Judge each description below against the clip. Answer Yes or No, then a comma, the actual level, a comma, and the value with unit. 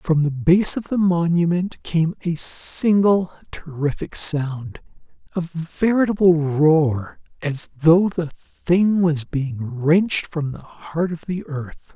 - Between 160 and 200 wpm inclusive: No, slow, 135 wpm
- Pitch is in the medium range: Yes, medium, 165 Hz